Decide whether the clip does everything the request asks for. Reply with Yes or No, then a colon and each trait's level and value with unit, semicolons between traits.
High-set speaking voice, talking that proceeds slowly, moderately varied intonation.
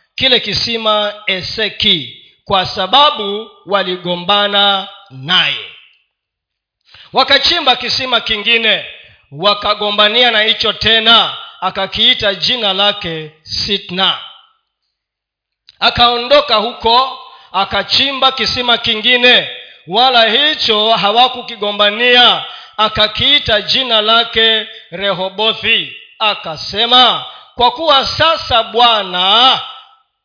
Yes: high, 220 Hz; slow, 70 wpm; average, 3.6 semitones